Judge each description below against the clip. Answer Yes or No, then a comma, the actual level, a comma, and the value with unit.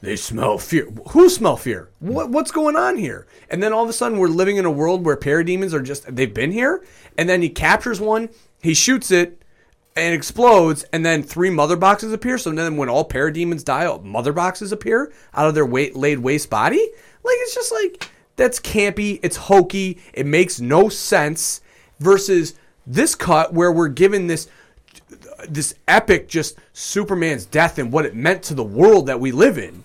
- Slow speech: No, average, 195 wpm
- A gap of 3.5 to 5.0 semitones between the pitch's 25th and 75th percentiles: No, wide, 5.4 semitones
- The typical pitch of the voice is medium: Yes, medium, 175 Hz